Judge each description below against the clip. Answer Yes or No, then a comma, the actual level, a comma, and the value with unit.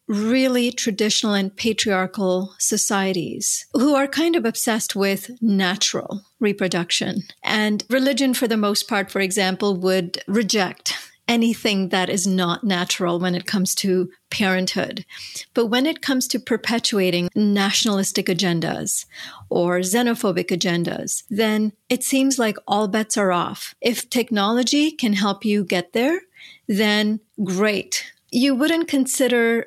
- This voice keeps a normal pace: No, slow, 130 wpm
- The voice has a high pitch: Yes, high, 210 Hz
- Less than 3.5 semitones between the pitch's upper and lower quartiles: No, average, 4.0 semitones